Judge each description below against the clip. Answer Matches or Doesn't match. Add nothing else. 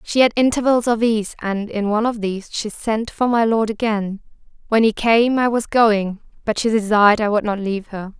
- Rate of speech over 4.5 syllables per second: Matches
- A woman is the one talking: Matches